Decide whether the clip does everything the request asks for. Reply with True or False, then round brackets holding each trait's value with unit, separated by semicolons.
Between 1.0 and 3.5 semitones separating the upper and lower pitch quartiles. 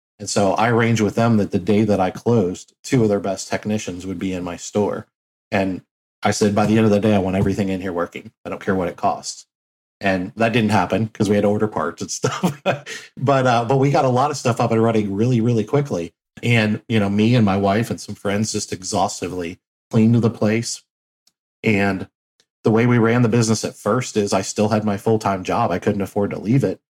True (2.5 semitones)